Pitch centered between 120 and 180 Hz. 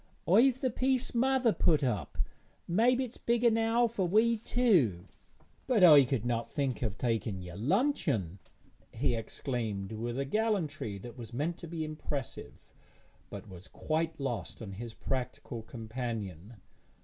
Yes: medium, 140 Hz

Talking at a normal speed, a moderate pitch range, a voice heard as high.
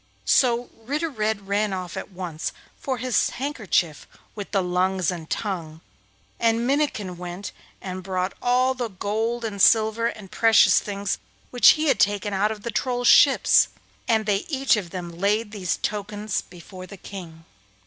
Yes: average, 160 wpm; average, 4.0 semitones; high, 205 Hz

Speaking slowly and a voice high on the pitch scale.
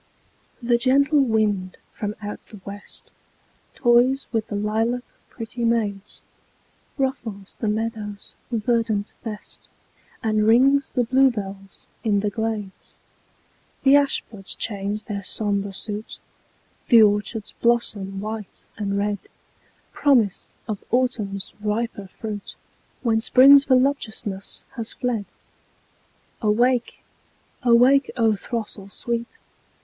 Yes: slow, 105 wpm; high, 220 Hz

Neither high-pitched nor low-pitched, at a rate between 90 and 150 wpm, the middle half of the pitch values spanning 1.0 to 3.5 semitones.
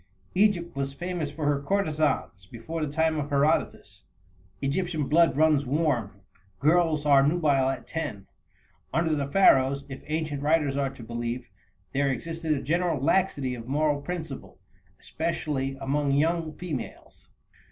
Yes: medium, 145 Hz; average, 140 wpm; average, 3.0 semitones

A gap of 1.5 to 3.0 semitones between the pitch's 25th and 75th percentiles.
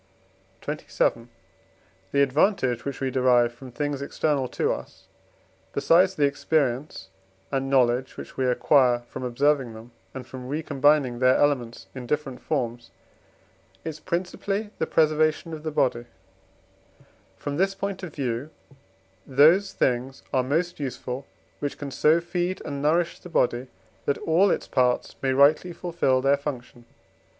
No: average, 3.7 semitones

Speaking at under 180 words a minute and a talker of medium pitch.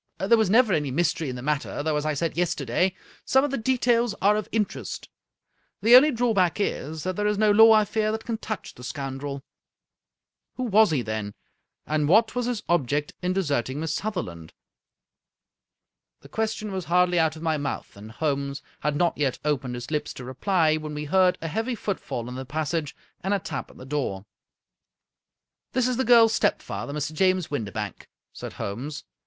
No: average, 195 wpm; medium, 165 Hz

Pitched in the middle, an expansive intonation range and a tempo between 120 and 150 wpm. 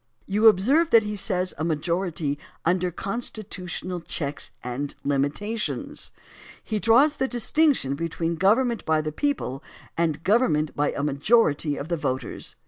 Yes: medium, 175 Hz; wide, 6.9 semitones; average, 140 wpm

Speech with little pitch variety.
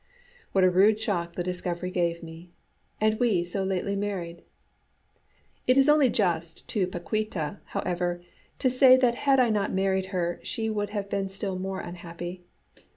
No: average, 3.5 semitones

